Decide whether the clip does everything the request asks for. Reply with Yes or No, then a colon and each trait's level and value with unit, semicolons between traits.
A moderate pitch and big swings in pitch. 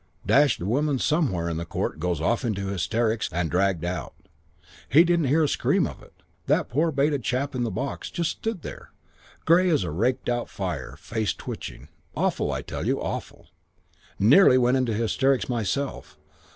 No: low, 120 Hz; wide, 7.1 semitones